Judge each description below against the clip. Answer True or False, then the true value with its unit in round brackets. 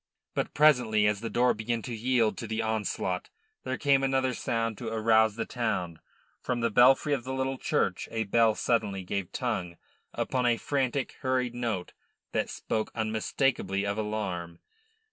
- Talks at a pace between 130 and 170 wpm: True (165 wpm)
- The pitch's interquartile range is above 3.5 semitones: False (2.9 semitones)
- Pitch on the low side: True (115 Hz)